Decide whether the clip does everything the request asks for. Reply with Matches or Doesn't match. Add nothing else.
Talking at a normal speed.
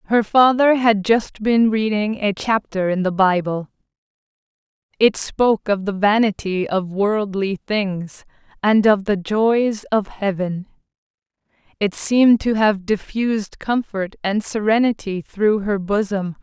Doesn't match